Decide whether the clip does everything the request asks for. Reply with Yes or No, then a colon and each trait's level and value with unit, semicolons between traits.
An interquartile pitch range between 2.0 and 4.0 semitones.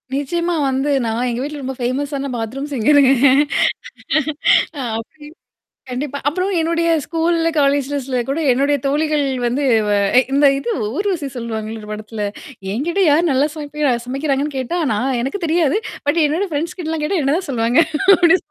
Yes: average, 3.5 semitones